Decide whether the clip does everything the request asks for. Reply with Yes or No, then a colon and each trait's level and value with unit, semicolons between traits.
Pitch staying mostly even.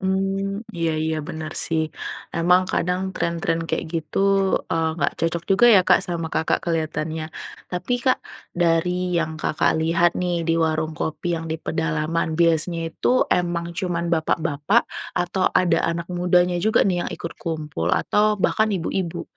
Yes: narrow, 1.9 semitones